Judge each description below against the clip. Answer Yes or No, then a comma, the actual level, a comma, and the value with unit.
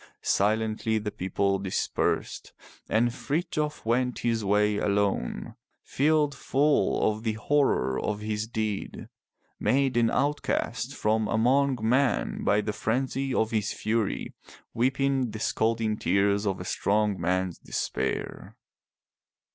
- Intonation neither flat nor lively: Yes, average, 3.9 semitones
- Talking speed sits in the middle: No, slow, 120 wpm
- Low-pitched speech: Yes, low, 110 Hz